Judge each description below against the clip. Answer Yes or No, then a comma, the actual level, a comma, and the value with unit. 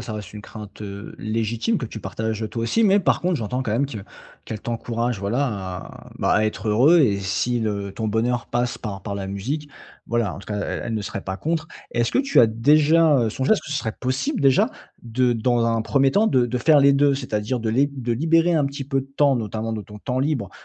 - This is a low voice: Yes, low, 120 Hz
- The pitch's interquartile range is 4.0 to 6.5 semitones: Yes, average, 4.5 semitones